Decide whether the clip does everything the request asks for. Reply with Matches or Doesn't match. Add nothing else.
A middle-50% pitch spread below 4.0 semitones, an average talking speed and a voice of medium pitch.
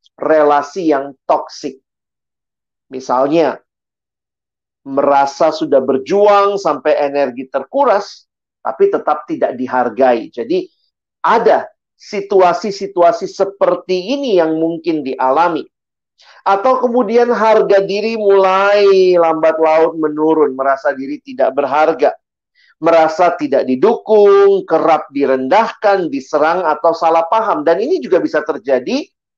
Doesn't match